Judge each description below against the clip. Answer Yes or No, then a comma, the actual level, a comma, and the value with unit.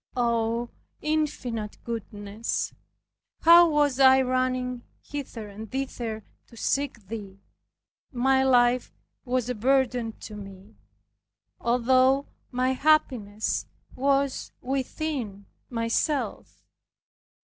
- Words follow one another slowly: Yes, slow, 90 wpm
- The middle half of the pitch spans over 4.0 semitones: No, average, 3.0 semitones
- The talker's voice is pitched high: Yes, very high, 250 Hz